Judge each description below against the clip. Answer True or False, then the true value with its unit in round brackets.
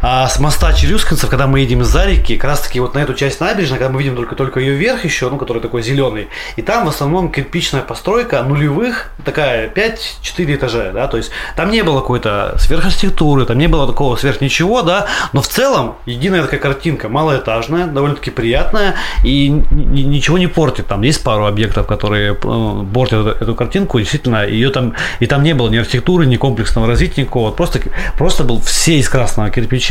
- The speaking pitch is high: False (135 Hz)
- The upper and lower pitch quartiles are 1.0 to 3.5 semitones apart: False (4.3 semitones)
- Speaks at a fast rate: True (195 wpm)